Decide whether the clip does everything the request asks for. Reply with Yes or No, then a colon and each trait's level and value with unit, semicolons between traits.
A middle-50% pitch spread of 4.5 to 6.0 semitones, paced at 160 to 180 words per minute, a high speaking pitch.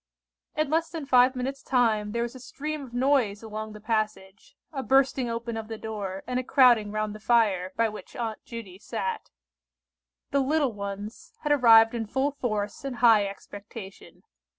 No: average, 3.7 semitones; average, 175 wpm; high, 230 Hz